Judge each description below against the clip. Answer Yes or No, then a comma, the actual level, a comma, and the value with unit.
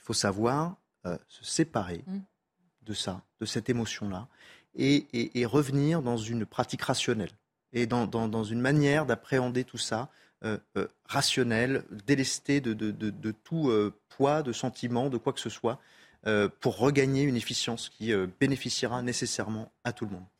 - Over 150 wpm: Yes, average, 175 wpm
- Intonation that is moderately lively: Yes, average, 3.6 semitones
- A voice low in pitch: Yes, low, 120 Hz